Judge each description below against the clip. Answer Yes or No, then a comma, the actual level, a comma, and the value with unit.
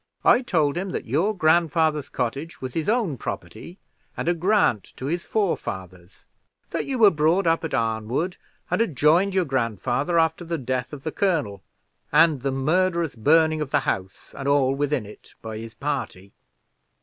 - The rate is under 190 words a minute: Yes, average, 175 wpm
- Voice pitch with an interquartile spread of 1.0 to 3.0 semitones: No, average, 4.9 semitones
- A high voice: No, medium, 150 Hz